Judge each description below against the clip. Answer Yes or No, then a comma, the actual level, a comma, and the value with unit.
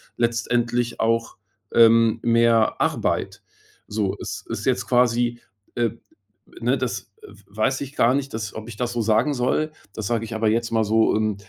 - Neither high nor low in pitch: No, low, 115 Hz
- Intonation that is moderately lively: No, narrow, 1.6 semitones